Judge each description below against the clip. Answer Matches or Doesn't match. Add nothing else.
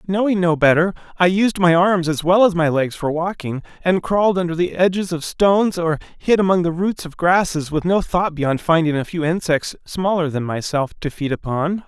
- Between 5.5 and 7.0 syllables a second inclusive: Doesn't match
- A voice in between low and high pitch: Matches